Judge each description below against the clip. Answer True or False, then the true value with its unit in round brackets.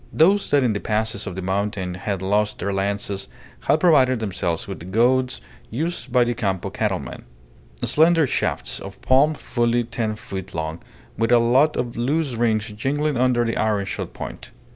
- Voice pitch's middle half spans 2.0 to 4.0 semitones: False (4.5 semitones)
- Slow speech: False (170 wpm)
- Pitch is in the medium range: False (115 Hz)